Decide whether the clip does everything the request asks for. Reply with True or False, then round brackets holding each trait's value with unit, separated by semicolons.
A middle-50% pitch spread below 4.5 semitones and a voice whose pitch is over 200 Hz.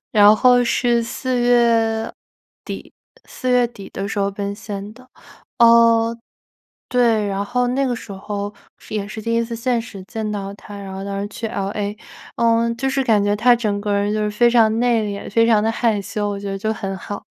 True (2.5 semitones; 220 Hz)